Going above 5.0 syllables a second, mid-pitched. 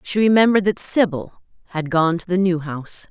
Yes: 5.6 syllables/s; medium, 180 Hz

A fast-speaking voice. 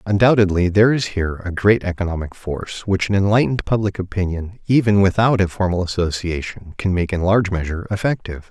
No: average, 170 wpm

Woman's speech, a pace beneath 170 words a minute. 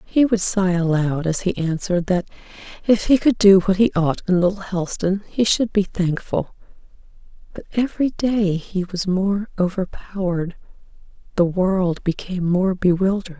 Yes: female; average, 150 wpm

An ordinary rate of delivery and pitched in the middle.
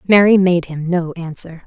Yes: average, 180 wpm; medium, 175 Hz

